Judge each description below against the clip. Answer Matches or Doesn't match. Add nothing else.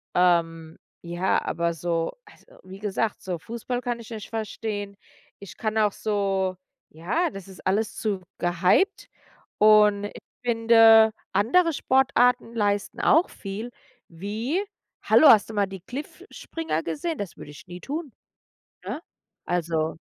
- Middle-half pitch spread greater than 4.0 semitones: Matches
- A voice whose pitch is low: Doesn't match